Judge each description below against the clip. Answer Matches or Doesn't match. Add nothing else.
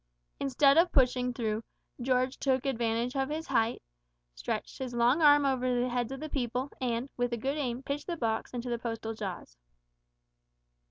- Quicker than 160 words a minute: Matches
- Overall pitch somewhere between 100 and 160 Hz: Doesn't match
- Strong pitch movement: Doesn't match